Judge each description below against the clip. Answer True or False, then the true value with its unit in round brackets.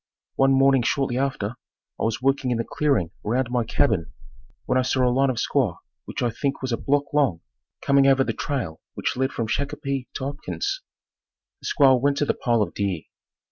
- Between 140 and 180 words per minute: False (200 wpm)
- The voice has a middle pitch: False (130 Hz)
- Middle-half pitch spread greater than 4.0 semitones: False (2.8 semitones)